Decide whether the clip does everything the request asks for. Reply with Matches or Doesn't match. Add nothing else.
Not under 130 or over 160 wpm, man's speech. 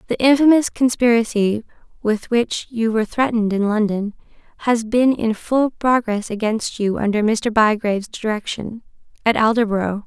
Doesn't match